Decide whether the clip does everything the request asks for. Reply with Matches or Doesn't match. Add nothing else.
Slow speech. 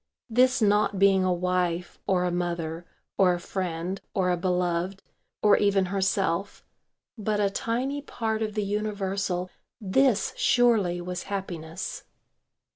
Matches